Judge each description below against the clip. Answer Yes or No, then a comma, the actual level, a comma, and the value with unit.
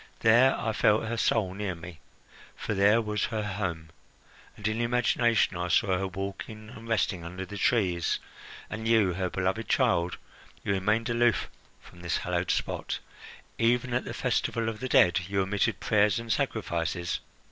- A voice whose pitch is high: No, low, 105 Hz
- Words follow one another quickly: No, average, 165 wpm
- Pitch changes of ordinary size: Yes, average, 3.7 semitones